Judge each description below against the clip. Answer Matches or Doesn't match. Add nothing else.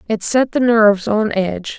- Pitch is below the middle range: Doesn't match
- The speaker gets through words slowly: Doesn't match